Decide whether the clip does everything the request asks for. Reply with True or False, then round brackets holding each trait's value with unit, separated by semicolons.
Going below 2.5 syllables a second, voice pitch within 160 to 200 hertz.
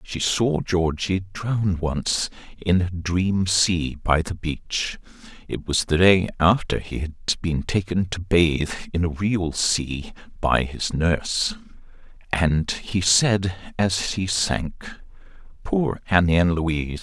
False (1.7 syllables/s; 90 Hz)